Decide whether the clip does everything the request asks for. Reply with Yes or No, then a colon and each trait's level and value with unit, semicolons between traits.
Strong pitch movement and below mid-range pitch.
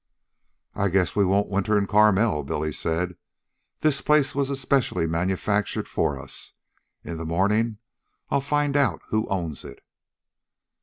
Yes: wide, 6.3 semitones; low, 100 Hz